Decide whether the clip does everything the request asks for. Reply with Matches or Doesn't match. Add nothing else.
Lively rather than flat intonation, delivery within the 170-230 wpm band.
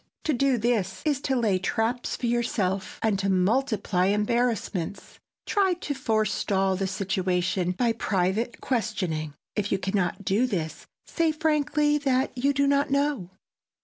Doesn't match